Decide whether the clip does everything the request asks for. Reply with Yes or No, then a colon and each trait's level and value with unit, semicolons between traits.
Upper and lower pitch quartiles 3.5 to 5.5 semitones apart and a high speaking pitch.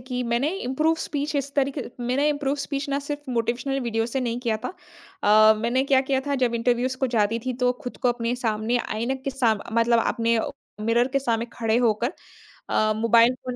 No: average, 2.8 semitones; high, 245 Hz